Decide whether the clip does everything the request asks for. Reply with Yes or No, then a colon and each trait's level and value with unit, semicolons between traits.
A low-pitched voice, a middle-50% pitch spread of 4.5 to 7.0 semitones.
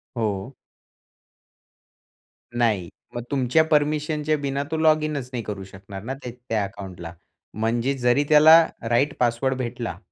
Yes: low, 125 Hz; average, 5.2 semitones